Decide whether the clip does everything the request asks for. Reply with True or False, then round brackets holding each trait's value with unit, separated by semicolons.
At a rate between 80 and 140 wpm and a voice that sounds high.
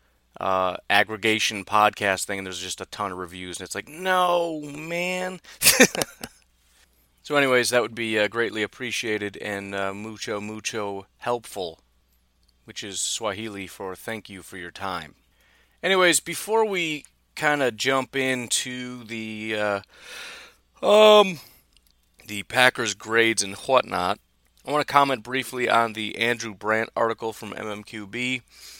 False (135 wpm; 110 Hz)